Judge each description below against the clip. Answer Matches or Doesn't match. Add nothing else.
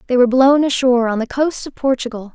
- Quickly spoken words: Matches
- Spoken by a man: Doesn't match